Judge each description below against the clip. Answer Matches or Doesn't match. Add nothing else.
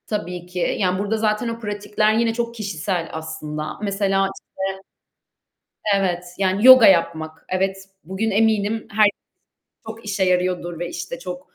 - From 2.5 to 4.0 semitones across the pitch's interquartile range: Matches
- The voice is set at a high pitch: Matches